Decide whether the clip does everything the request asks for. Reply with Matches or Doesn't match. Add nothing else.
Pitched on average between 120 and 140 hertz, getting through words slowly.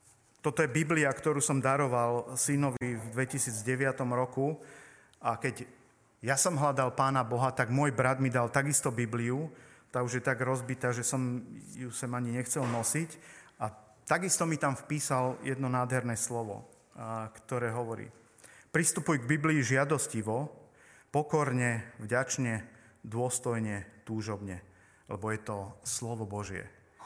Doesn't match